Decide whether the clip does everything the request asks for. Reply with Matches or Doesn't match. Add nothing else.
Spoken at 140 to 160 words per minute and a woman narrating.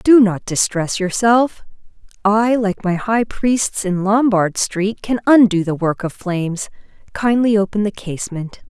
Matches